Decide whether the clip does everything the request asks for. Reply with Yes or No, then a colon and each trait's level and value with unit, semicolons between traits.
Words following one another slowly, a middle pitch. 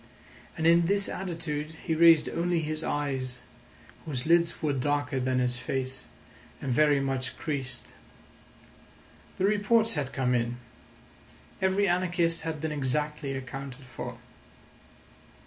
Yes: slow, 125 wpm; medium, 150 Hz